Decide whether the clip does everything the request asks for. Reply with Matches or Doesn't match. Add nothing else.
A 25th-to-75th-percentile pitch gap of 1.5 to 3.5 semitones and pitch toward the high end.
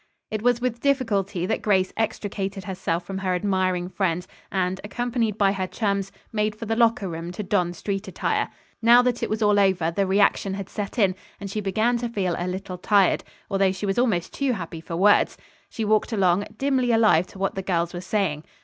Matches